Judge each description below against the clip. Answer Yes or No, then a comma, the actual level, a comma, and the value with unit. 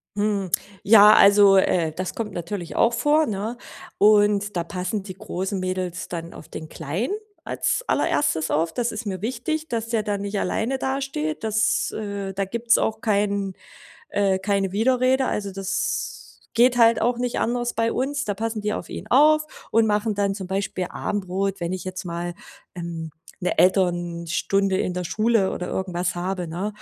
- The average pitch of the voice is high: Yes, high, 200 Hz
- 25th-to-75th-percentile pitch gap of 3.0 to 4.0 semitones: Yes, average, 3.7 semitones